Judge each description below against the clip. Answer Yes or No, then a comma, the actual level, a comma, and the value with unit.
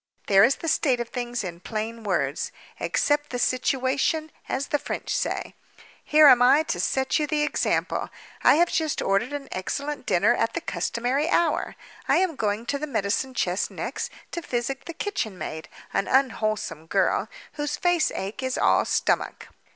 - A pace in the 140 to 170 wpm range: Yes, average, 165 wpm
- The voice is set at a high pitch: Yes, very high, 260 Hz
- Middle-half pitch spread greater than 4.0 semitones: Yes, wide, 5.5 semitones